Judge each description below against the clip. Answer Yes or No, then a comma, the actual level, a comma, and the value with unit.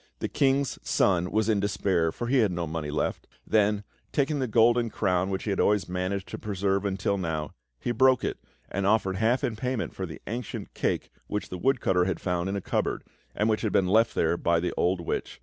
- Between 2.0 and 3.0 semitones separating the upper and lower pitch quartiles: No, average, 3.7 semitones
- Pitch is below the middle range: Yes, low, 100 Hz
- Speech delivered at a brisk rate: Yes, fast, 220 wpm